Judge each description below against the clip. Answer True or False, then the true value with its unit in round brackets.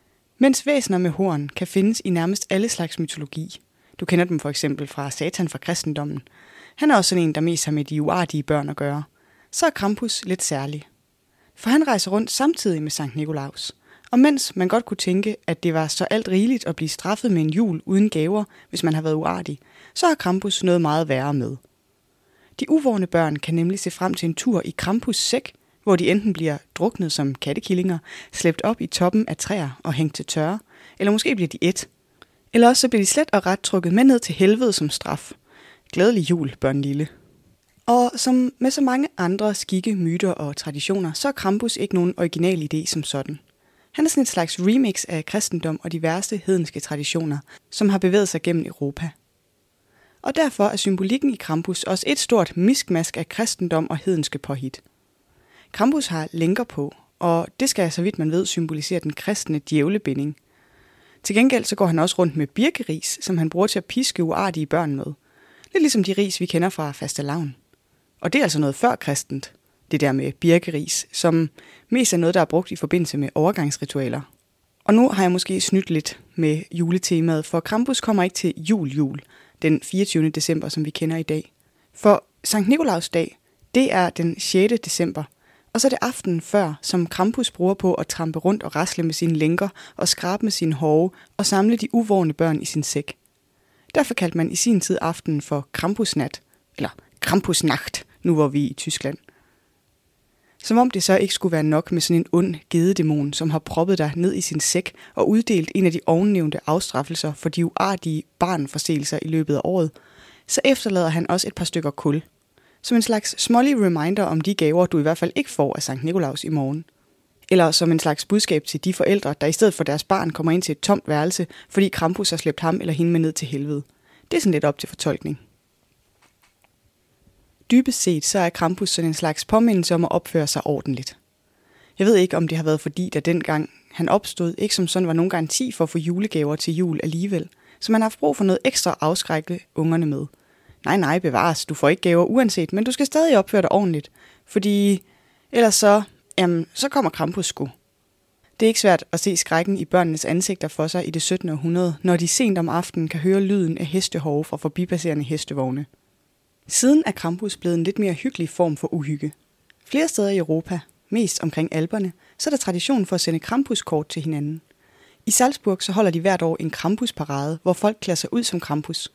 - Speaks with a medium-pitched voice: True (170 Hz)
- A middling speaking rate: True (205 wpm)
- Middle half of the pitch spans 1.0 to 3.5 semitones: False (4.2 semitones)